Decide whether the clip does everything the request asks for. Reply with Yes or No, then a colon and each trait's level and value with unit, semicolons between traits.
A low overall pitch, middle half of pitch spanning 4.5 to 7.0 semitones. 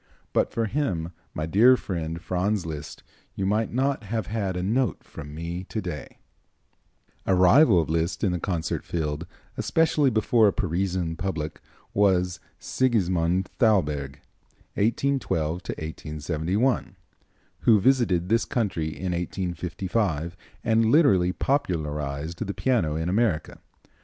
Yes: very low, 90 Hz; average, 5.1 semitones